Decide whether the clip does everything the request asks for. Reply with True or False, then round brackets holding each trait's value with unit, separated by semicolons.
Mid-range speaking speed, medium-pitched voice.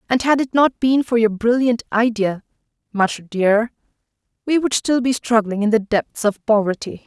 False (180 wpm; 225 Hz)